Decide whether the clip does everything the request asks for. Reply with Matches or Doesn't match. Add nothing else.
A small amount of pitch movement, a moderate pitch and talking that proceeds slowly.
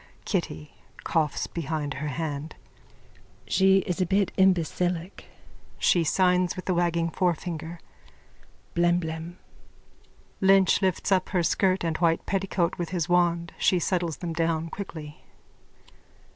Matches